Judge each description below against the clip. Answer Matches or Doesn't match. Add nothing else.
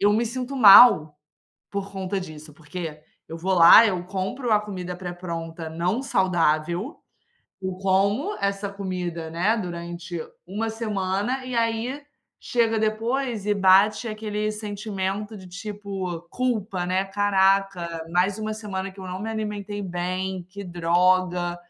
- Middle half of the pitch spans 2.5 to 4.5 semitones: Matches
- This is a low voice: Doesn't match